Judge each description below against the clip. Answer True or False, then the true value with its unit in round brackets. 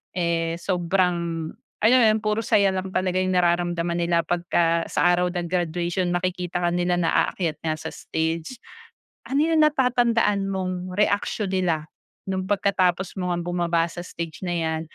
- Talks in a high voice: False (175 Hz)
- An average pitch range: False (1.9 semitones)